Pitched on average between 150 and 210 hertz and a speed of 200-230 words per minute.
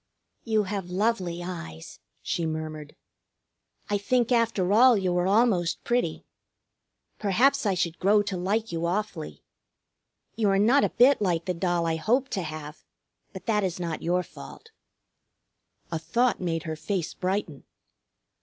No: high, 190 Hz; average, 150 wpm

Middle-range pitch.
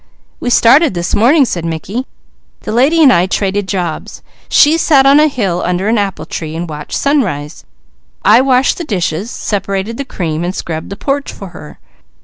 No: high, 200 Hz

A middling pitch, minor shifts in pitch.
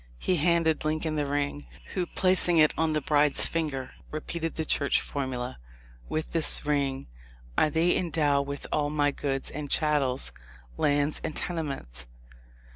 Yes: medium, 150 Hz; narrow, 2.1 semitones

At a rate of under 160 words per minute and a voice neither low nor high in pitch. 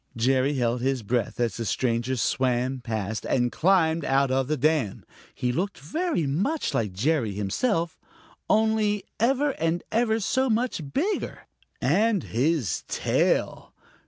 Yes: average, 140 wpm; medium, 145 Hz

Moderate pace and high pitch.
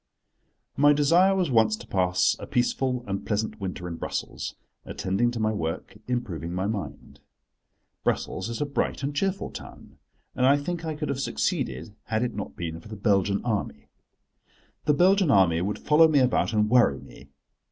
No: average, 175 wpm; low, 110 Hz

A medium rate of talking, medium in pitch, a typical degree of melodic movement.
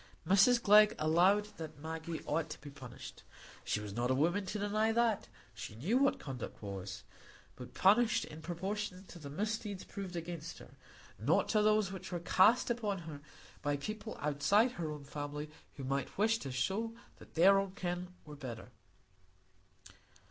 No: average, 160 wpm; medium, 175 Hz; wide, 6.1 semitones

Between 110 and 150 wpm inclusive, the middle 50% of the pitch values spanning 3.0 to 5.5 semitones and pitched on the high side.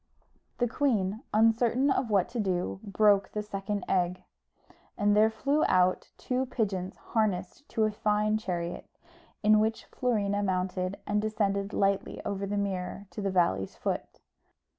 No: average, 140 wpm; narrow, 2.6 semitones; high, 205 Hz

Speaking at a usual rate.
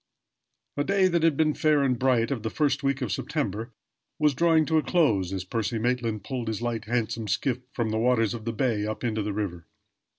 No: fast, 220 wpm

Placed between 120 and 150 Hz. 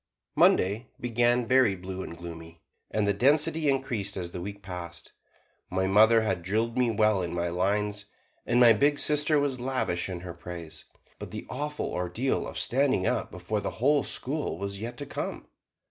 No: low, 105 Hz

